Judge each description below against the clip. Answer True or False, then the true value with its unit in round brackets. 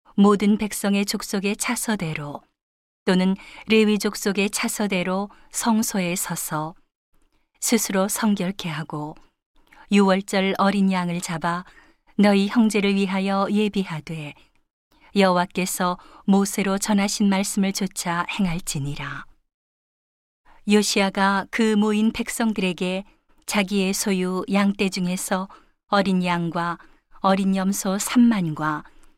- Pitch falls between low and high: False (195 Hz)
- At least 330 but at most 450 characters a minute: False (225 characters per minute)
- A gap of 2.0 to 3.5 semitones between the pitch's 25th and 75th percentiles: True (2.4 semitones)